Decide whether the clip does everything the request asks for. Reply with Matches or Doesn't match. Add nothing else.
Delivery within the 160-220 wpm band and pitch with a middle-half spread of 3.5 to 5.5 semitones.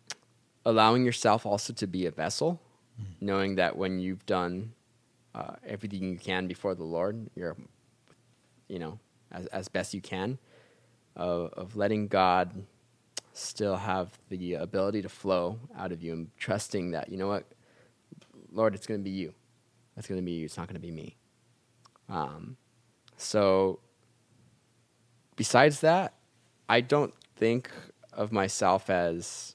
Doesn't match